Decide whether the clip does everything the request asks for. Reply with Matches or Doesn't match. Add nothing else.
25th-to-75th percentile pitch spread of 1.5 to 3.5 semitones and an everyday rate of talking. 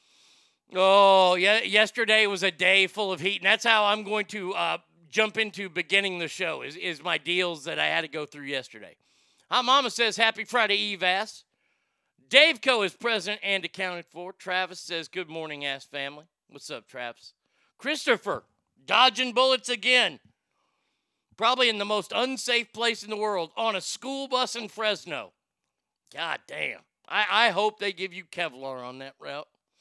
Doesn't match